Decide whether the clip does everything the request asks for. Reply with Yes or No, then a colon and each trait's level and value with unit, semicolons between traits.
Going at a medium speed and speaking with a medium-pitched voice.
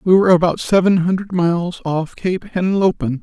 Yes: average, 165 wpm; medium, 175 Hz